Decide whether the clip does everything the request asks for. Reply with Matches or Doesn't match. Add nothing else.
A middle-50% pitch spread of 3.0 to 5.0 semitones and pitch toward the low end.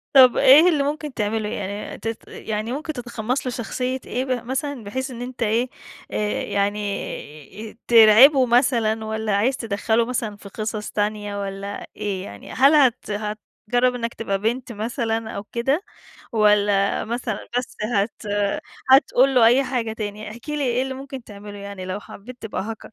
Doesn't match